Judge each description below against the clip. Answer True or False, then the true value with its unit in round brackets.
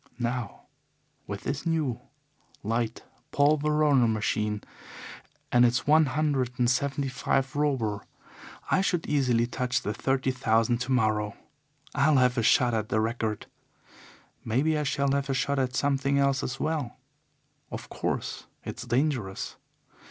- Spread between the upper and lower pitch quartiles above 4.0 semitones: False (3.2 semitones)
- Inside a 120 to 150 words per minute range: True (135 wpm)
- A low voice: True (130 Hz)